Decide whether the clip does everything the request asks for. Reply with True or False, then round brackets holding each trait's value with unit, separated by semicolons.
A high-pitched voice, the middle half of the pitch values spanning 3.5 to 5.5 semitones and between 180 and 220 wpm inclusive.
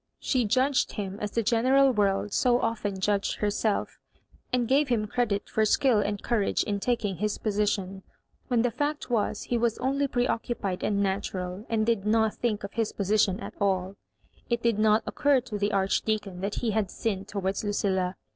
False (215 Hz; 3.0 semitones; 185 wpm)